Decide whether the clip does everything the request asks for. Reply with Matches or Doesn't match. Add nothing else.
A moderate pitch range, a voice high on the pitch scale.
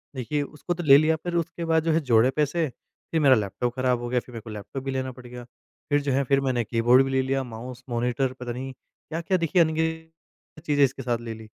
Doesn't match